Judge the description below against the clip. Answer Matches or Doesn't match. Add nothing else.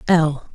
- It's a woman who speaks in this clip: Doesn't match